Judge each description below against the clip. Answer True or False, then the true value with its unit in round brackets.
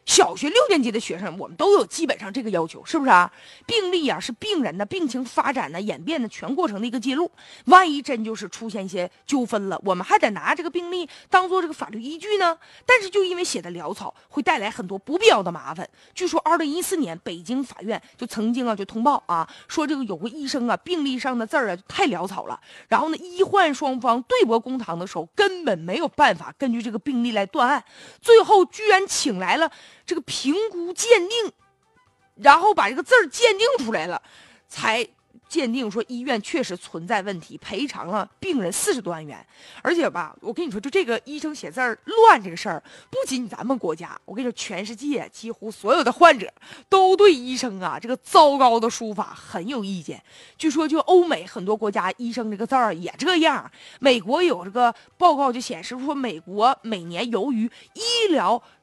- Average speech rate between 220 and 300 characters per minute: False (310 characters per minute)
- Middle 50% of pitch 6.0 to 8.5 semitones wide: True (7.2 semitones)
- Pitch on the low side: False (265 Hz)